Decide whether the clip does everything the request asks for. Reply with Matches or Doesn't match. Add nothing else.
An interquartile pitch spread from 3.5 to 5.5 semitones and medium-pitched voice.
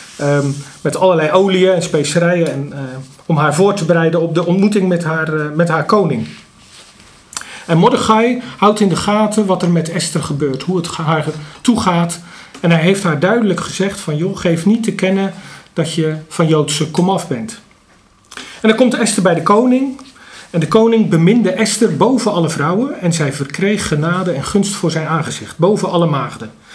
Matches